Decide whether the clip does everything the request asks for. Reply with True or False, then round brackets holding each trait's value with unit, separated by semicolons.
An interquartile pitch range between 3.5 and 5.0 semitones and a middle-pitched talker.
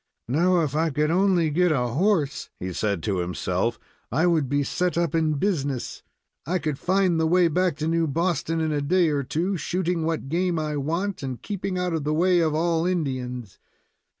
True (3.9 semitones; 160 Hz)